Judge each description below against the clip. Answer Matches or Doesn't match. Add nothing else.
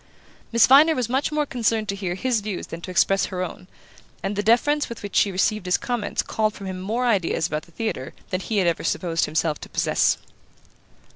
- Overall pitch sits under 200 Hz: Doesn't match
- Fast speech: Matches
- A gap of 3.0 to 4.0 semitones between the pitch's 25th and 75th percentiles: Doesn't match